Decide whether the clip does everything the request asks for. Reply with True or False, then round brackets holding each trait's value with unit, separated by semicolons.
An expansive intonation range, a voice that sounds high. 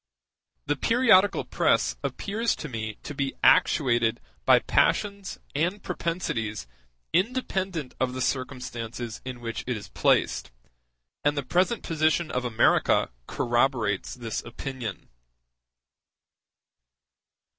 False (6.9 semitones; 135 Hz)